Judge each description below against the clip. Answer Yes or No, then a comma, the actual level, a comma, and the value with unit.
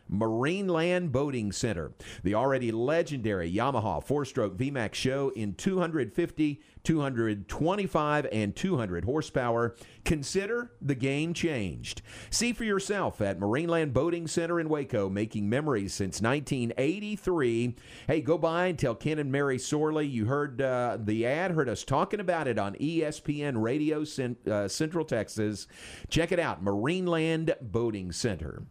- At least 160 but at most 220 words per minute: No, average, 140 wpm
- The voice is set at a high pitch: No, low, 135 Hz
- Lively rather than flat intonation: Yes, wide, 6.8 semitones